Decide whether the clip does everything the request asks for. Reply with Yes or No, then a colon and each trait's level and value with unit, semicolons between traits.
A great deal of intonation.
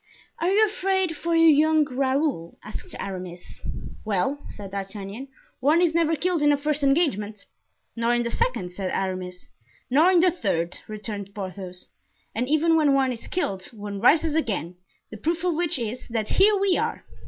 Yes: wide, 8.4 semitones